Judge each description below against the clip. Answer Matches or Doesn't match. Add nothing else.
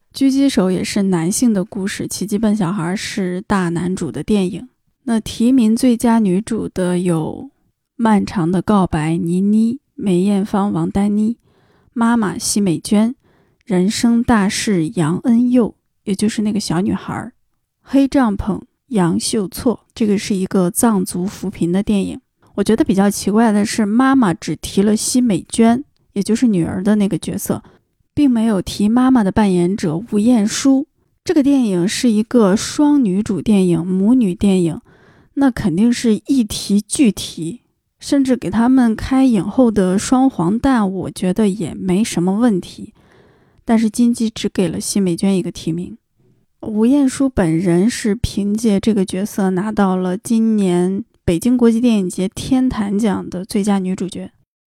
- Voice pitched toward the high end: Matches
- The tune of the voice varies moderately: Matches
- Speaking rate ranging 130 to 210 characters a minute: Doesn't match